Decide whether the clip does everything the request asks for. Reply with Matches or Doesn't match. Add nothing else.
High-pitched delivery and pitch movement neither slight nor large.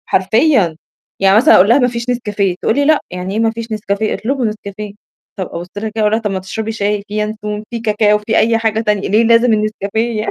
Doesn't match